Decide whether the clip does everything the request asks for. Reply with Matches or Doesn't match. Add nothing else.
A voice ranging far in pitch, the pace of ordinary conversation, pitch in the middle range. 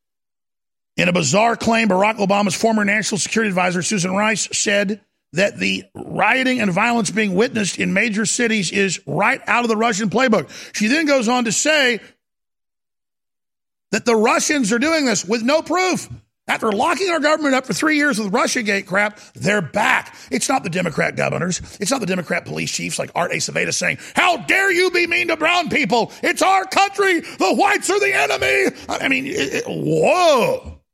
Doesn't match